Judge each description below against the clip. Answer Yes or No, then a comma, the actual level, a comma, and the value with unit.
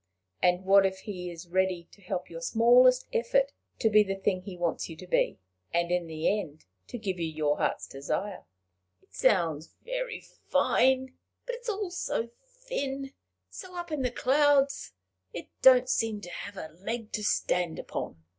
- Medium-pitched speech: No, high, 205 Hz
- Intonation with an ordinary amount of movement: No, wide, 6.9 semitones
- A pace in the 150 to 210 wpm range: Yes, average, 175 wpm